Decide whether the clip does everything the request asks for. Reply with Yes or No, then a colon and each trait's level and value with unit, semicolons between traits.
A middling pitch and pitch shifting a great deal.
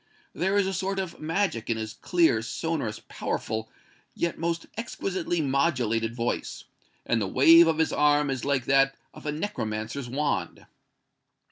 Yes: medium, 145 Hz; wide, 6.5 semitones